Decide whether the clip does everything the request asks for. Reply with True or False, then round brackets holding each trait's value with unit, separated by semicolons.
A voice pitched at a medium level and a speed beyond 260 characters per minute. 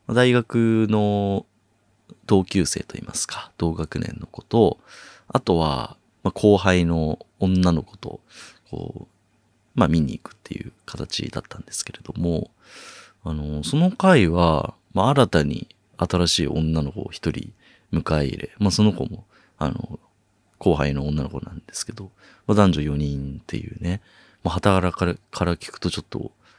False (90 Hz; 270 characters per minute)